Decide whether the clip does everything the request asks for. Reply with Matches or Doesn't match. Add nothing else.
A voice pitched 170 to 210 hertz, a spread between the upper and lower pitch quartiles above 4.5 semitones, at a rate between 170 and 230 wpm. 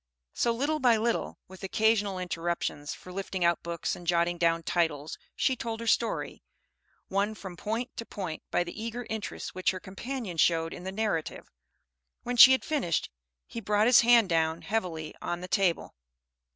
Matches